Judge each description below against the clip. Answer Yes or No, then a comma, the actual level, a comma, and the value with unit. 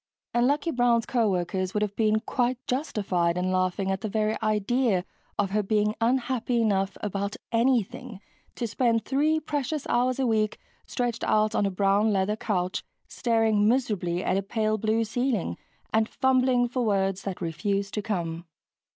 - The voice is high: Yes, high, 215 Hz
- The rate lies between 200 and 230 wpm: No, average, 165 wpm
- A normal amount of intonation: Yes, average, 3.7 semitones